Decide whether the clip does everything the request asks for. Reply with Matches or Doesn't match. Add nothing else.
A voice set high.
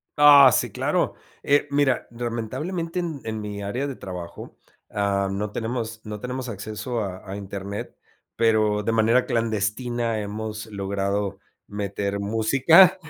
Doesn't match